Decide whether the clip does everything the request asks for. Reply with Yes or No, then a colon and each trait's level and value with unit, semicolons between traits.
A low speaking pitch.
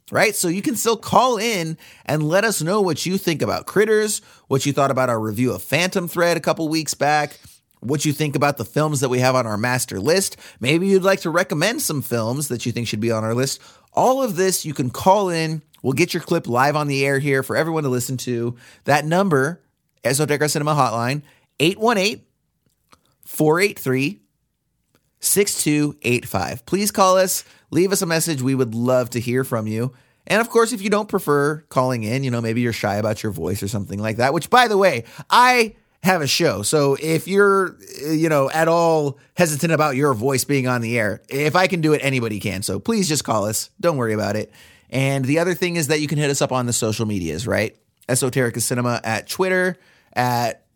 No: medium, 145 Hz